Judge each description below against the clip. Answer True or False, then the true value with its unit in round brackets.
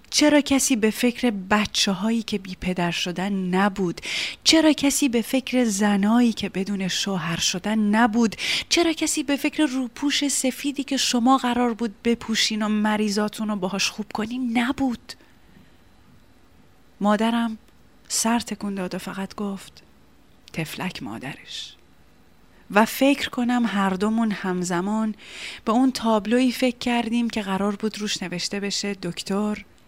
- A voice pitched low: False (215 Hz)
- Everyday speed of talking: True (135 wpm)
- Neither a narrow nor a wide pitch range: True (4.0 semitones)